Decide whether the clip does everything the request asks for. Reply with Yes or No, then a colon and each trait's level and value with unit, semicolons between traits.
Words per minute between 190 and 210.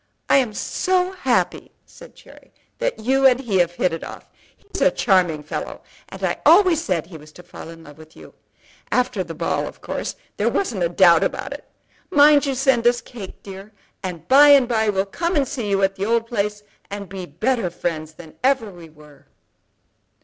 Yes: average, 200 wpm